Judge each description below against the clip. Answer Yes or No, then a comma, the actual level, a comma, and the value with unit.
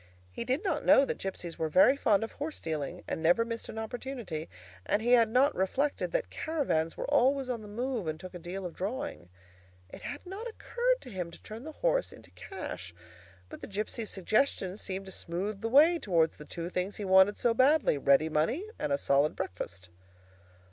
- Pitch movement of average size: No, wide, 8.0 semitones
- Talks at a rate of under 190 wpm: No, average, 200 wpm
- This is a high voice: Yes, high, 215 Hz